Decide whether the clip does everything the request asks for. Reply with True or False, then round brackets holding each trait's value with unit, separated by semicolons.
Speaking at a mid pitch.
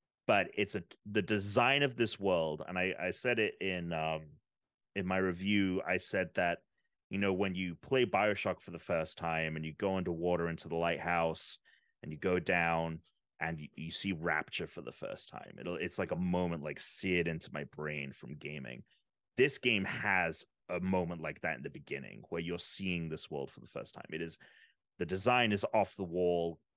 False (90 Hz)